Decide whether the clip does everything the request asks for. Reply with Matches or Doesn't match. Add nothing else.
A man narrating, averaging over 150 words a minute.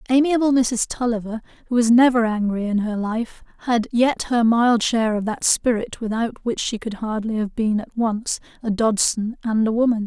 Doesn't match